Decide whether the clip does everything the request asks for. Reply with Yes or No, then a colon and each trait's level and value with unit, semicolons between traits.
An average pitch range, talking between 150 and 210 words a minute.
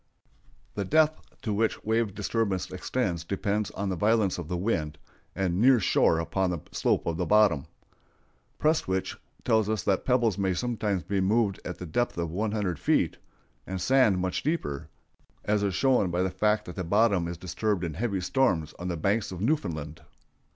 Yes: average, 3.7 semitones; average, 180 wpm